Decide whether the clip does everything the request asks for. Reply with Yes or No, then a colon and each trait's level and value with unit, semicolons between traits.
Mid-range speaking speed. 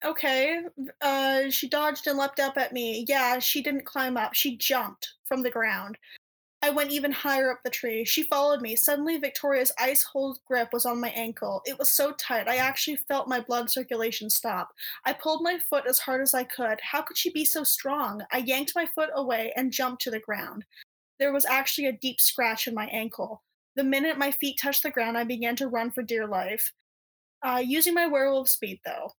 No: fast, 210 wpm